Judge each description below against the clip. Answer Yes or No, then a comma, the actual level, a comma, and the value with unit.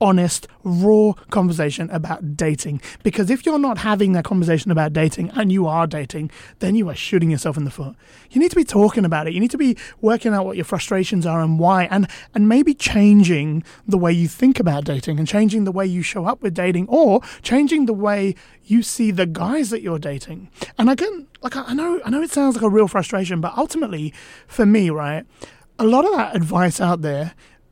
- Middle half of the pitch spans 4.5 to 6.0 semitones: Yes, wide, 5.4 semitones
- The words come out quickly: Yes, fast, 220 wpm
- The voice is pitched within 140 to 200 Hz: Yes, high, 190 Hz